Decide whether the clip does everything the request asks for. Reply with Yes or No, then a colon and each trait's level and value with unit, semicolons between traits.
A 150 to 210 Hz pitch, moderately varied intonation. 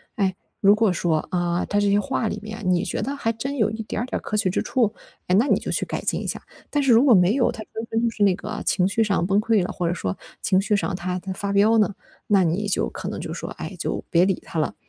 Yes: high, 205 Hz; average, 3.4 semitones